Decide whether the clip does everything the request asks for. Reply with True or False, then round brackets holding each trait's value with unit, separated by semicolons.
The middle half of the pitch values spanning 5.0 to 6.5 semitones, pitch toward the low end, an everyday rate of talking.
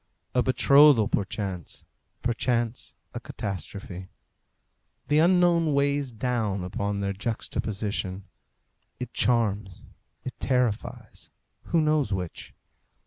False (5.6 semitones; 115 Hz; 90 wpm)